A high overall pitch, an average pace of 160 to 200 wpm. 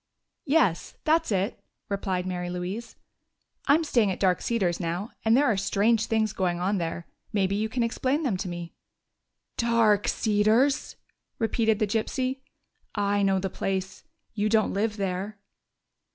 No: high, 210 Hz; average, 140 wpm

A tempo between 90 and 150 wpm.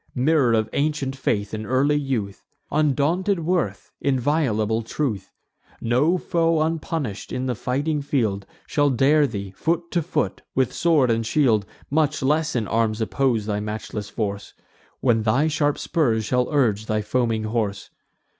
Yes: average, 145 wpm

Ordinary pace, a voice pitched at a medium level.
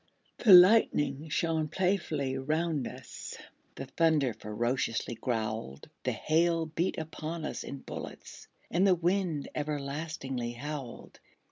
No: slow, 115 wpm; medium, 155 Hz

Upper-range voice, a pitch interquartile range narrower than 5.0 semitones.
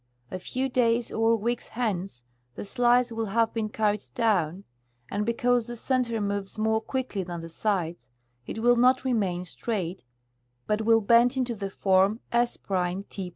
Yes: high, 220 Hz; average, 3.5 semitones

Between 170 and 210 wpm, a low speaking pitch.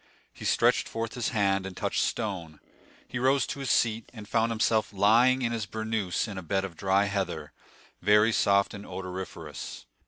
Yes: average, 180 wpm; low, 105 Hz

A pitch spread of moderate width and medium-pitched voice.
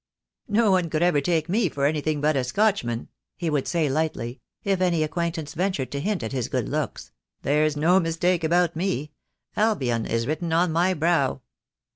Yes: average, 3.9 semitones; medium, 160 Hz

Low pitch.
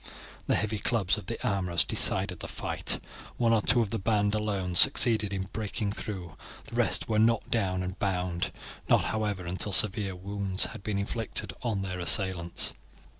Yes: low, 100 Hz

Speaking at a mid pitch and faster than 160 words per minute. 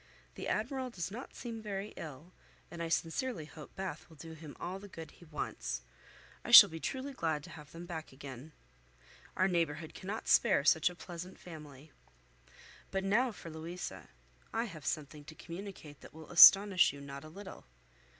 Yes: medium, 170 Hz; average, 180 wpm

